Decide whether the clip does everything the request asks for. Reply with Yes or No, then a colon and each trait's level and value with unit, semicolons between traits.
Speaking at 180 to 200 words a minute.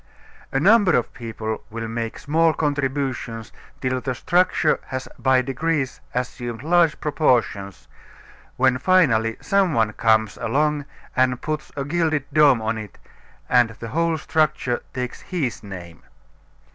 No: slow, 135 wpm